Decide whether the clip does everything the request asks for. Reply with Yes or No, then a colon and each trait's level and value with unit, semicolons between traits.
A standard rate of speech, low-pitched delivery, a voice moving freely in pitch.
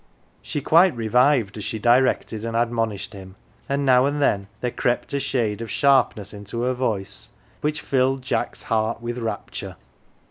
No: average, 165 wpm; low, 120 Hz; average, 3.4 semitones